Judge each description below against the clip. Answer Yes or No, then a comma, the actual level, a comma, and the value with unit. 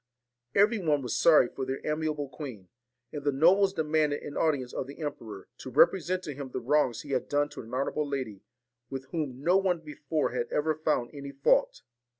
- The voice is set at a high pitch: No, medium, 145 Hz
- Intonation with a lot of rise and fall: No, average, 3.1 semitones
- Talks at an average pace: Yes, average, 195 wpm